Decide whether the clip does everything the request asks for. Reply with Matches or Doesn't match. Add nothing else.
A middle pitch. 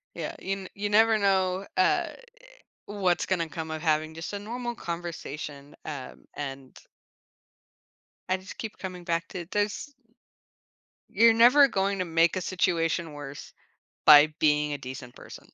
Matches